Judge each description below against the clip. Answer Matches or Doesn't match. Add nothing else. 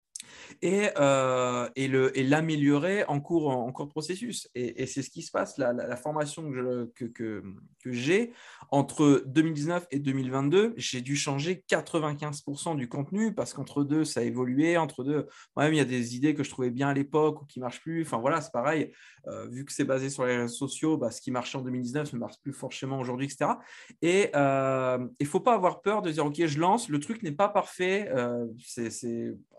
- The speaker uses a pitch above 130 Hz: Matches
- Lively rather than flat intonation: Doesn't match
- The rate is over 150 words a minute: Matches